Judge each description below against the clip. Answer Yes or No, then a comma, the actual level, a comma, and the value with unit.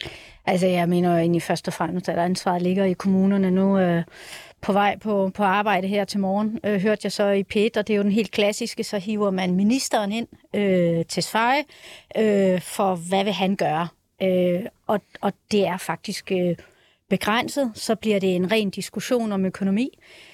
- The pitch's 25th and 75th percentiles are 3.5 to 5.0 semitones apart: No, narrow, 2.5 semitones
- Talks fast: No, average, 170 wpm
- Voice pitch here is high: Yes, high, 195 Hz